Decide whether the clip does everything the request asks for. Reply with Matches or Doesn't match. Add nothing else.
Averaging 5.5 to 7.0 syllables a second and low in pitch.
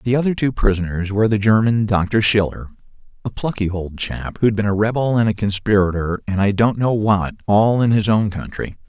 Doesn't match